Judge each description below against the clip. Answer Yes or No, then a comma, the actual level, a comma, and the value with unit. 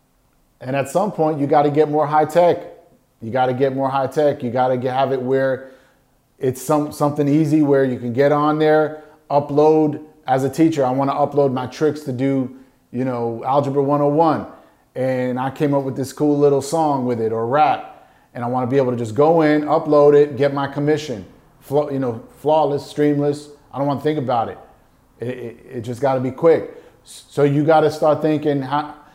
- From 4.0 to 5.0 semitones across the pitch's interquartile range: No, narrow, 2.6 semitones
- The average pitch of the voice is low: No, medium, 145 Hz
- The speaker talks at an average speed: No, fast, 210 wpm